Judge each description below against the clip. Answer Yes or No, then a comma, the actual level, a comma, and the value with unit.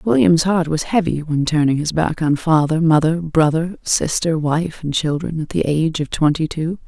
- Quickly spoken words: No, average, 190 wpm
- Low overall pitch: No, medium, 160 Hz